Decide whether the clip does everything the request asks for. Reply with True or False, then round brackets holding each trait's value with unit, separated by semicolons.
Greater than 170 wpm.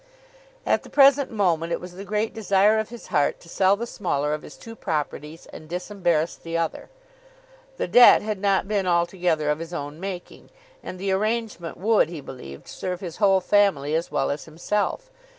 True (185 wpm)